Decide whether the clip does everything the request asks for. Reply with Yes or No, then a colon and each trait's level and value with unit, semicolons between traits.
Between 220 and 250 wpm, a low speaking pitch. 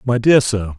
Yes: fast, 230 wpm; low, 110 Hz